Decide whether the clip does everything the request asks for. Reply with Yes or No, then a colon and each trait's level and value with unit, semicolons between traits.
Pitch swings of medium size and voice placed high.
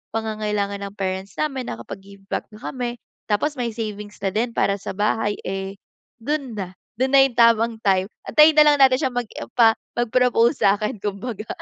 Yes: average, 3.7 semitones; high, 220 Hz